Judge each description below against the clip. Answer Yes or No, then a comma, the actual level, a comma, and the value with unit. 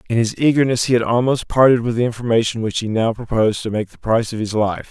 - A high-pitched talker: No, low, 115 Hz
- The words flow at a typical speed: No, fast, 255 wpm